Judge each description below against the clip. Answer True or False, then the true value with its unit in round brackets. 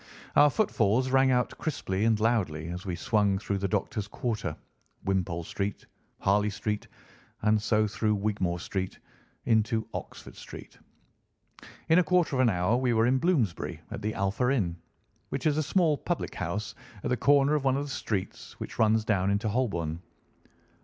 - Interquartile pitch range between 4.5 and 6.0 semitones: True (4.9 semitones)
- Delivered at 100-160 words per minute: False (170 wpm)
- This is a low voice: True (110 Hz)